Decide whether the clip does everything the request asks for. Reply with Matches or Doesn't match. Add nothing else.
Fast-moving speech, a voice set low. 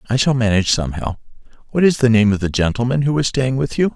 Matches